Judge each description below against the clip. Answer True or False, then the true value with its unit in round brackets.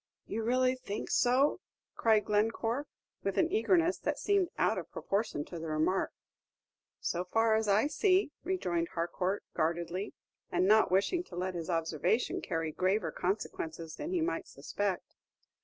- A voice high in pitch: True (205 Hz)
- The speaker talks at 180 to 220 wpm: False (150 wpm)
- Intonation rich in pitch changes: True (6.6 semitones)